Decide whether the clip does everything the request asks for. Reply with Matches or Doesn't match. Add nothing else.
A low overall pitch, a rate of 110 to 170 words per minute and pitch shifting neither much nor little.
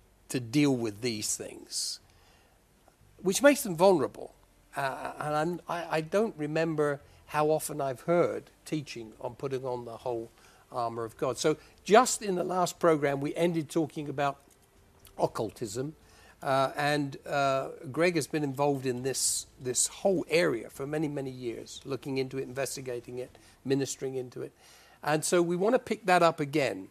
Doesn't match